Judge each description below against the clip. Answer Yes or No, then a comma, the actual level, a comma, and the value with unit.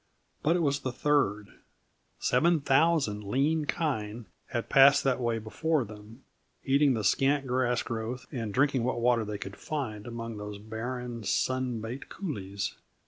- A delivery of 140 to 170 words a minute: Yes, average, 150 wpm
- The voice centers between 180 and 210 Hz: No, low, 125 Hz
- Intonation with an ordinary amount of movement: Yes, average, 4.0 semitones